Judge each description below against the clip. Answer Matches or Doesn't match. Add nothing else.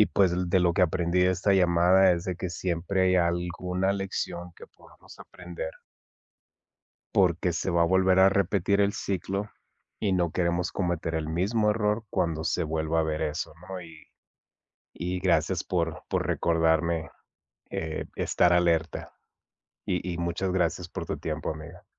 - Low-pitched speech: Matches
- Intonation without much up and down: Matches